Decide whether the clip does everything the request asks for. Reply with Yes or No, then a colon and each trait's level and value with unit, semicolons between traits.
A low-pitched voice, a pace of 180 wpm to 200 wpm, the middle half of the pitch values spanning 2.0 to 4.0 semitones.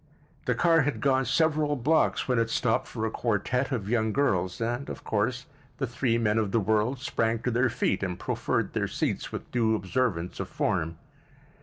Yes: low, 115 Hz; average, 190 wpm; average, 3.5 semitones